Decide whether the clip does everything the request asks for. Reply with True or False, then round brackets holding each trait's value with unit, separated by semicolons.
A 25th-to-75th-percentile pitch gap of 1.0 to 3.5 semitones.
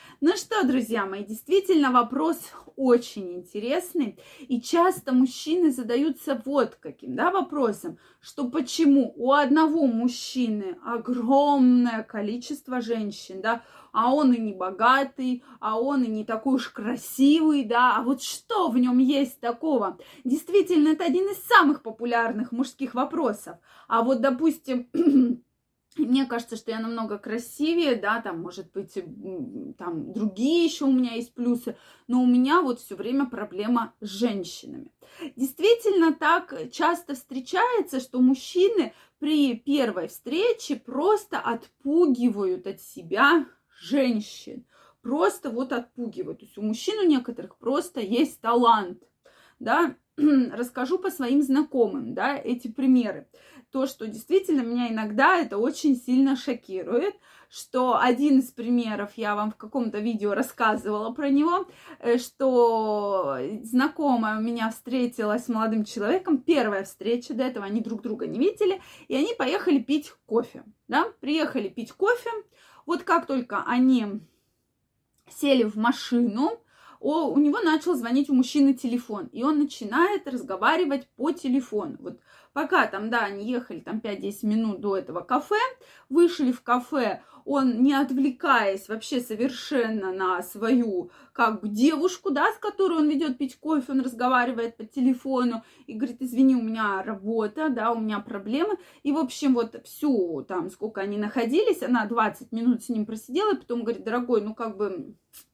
False (4.5 semitones)